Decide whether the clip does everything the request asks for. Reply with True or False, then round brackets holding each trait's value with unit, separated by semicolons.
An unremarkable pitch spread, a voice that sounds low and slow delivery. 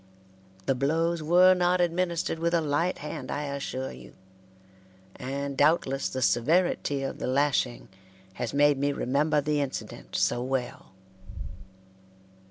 False (3.6 semitones; 145 Hz; 130 wpm)